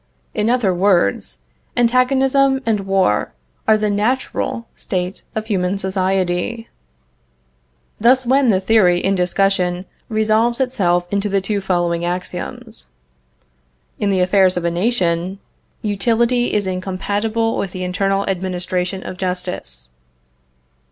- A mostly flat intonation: No, average, 3.6 semitones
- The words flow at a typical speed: No, slow, 120 wpm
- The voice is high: Yes, high, 195 Hz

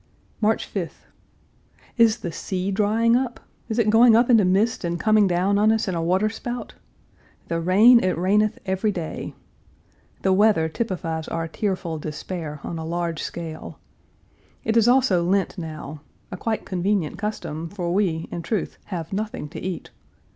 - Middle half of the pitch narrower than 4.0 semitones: No, average, 4.3 semitones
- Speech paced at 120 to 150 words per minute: No, average, 160 wpm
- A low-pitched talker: No, high, 190 Hz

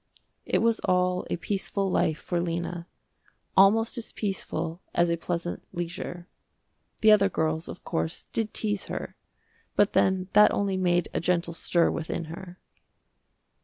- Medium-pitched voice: Yes, medium, 180 Hz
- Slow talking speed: No, average, 145 wpm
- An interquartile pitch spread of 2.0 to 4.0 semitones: Yes, narrow, 2.6 semitones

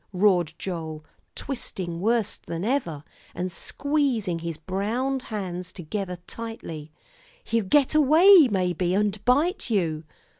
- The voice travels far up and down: Yes, wide, 6.3 semitones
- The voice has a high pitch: Yes, high, 195 Hz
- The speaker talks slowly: Yes, slow, 115 wpm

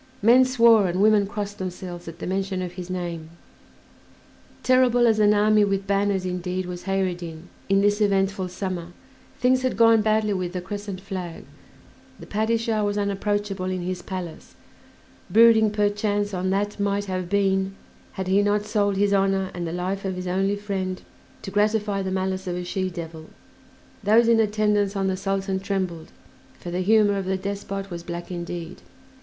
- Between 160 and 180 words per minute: Yes, average, 175 wpm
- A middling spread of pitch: No, narrow, 2.0 semitones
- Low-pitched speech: No, high, 195 Hz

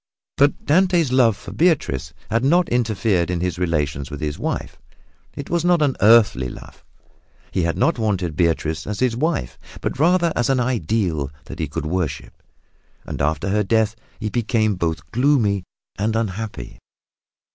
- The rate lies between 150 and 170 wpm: Yes, average, 160 wpm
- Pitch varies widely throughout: Yes, wide, 7.1 semitones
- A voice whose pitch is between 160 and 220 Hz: No, low, 110 Hz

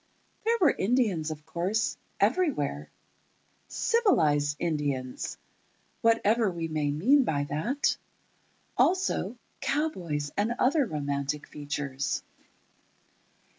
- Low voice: No, medium, 170 Hz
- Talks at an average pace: No, slow, 85 wpm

